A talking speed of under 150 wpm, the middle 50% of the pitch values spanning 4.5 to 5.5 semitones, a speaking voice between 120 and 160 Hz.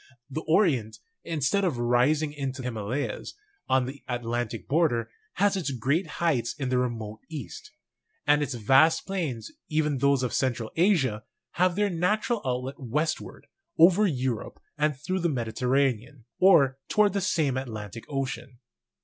Yes: average, 140 wpm; average, 5.0 semitones; low, 135 Hz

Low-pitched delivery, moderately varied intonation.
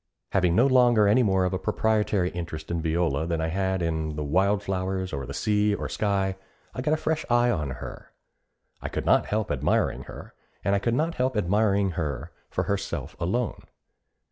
Yes: very low, 95 Hz; average, 4.3 semitones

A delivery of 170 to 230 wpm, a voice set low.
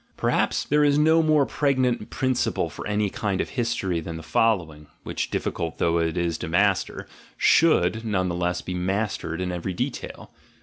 Yes: average, 180 wpm; very low, 95 Hz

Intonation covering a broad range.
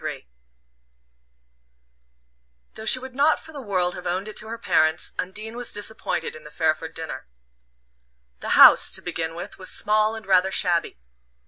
No: average, 4.6 semitones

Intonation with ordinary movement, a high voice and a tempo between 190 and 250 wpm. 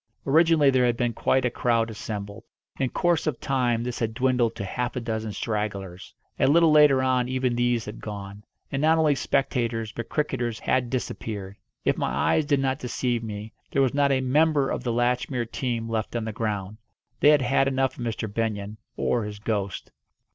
No: average, 3.3 semitones; low, 120 Hz; average, 195 wpm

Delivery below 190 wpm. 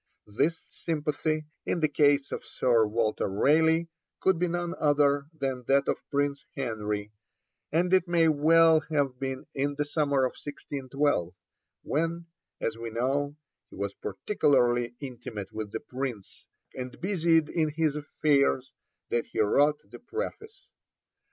Yes: average, 140 wpm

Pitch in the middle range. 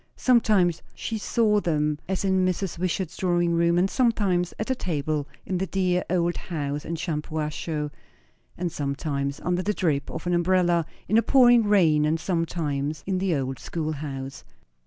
Yes: medium, 175 Hz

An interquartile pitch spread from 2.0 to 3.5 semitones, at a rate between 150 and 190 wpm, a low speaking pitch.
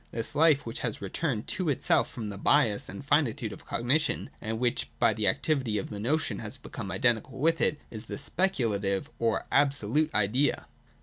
No: wide, 5.4 semitones; average, 180 wpm; low, 120 Hz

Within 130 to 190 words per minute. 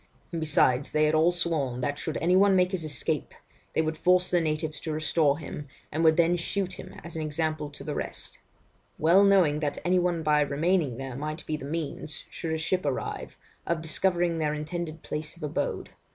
No: fast, 205 wpm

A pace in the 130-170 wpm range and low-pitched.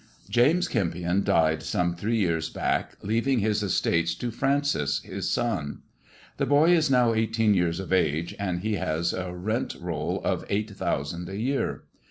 Yes: average, 165 wpm; low, 100 Hz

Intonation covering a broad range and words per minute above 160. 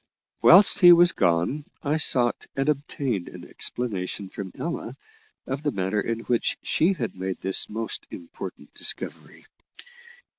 No: wide, 7.5 semitones; average, 140 wpm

